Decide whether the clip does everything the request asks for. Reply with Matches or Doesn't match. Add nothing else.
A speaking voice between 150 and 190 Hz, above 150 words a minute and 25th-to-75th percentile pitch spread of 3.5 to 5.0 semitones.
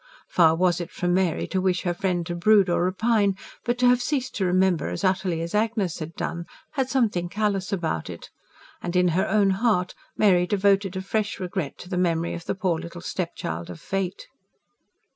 Doesn't match